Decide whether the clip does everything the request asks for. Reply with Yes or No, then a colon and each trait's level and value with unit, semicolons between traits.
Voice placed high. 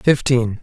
No: low, 125 Hz